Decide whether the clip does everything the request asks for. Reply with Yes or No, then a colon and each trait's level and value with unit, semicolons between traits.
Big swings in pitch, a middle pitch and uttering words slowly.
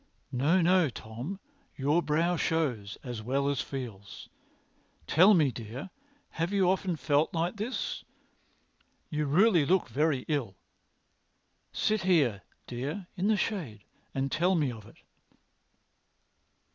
Yes: wide, 6.0 semitones; medium, 150 Hz; slow, 125 wpm